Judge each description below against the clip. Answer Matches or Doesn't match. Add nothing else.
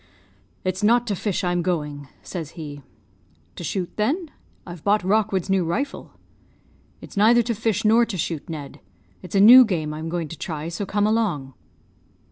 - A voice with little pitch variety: Doesn't match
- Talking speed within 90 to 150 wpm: Doesn't match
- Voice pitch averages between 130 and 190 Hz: Matches